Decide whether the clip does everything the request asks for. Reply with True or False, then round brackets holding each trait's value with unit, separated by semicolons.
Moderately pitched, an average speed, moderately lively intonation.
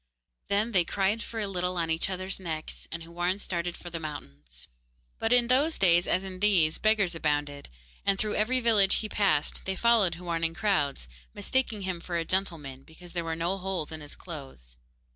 True (180 Hz; 195 wpm; 3.6 semitones)